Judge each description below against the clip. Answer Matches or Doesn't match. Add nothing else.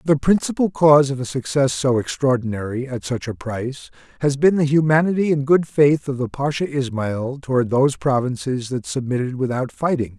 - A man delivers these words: Matches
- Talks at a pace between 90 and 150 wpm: Doesn't match